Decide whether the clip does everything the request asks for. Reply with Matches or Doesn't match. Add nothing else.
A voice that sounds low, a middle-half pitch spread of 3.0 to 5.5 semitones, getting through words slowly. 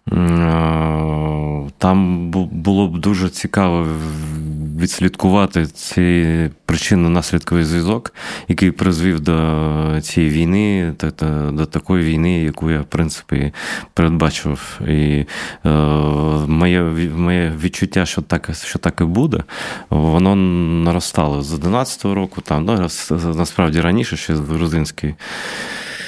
Doesn't match